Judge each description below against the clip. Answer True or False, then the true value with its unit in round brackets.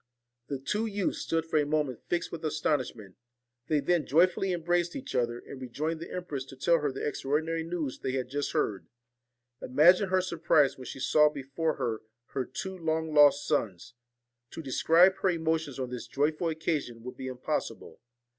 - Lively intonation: False (4.0 semitones)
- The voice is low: False (150 Hz)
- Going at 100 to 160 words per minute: False (175 wpm)